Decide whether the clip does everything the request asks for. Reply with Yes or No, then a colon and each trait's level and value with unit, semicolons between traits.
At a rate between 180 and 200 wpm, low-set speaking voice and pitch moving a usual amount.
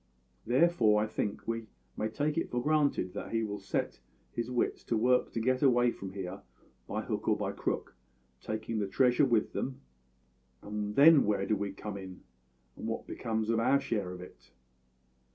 Yes: average, 185 wpm; low, 115 Hz; average, 3.5 semitones